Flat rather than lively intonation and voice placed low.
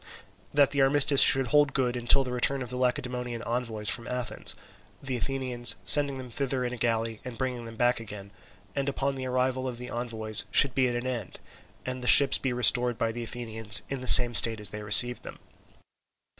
Yes: narrow, 2.2 semitones; low, 125 Hz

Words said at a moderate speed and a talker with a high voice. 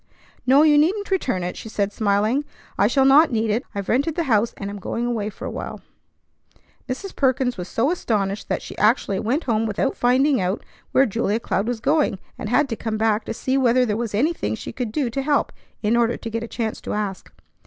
No: fast, 225 wpm; high, 235 Hz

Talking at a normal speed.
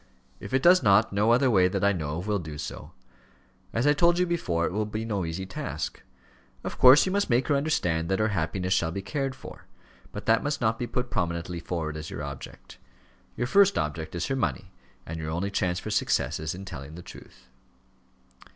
No: fast, 215 wpm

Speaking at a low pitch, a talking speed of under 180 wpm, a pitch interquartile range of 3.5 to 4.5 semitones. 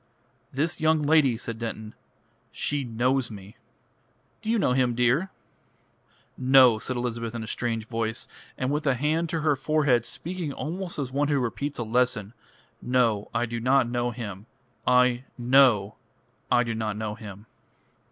Yes: low, 125 Hz; average, 160 wpm; average, 3.8 semitones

